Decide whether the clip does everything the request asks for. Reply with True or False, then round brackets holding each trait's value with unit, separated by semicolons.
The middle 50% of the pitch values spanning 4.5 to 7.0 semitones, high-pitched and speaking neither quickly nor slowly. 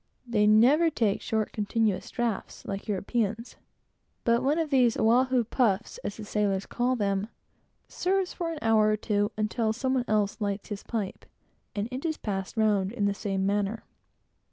False (3.2 semitones; 215 Hz; 170 wpm)